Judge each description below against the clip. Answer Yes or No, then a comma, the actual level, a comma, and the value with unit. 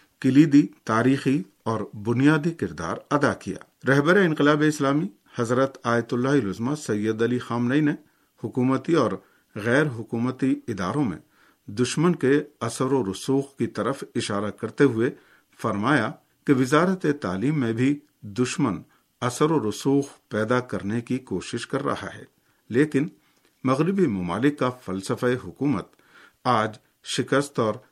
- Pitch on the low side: Yes, low, 130 Hz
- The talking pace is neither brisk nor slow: Yes, average, 130 wpm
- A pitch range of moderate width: Yes, average, 3.9 semitones